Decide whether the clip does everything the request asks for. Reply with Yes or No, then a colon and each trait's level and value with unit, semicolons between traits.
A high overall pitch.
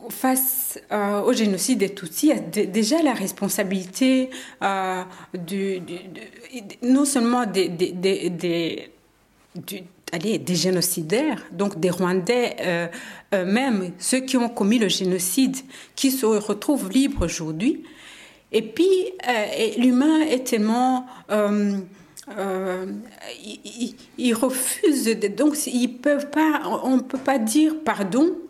Yes: high, 220 Hz